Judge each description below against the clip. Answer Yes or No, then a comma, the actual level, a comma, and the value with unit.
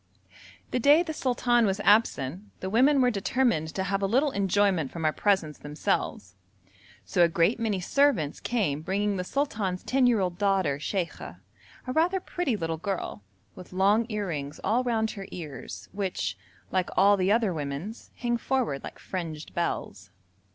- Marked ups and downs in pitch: Yes, wide, 5.8 semitones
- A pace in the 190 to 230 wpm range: No, average, 165 wpm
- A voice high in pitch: Yes, high, 195 Hz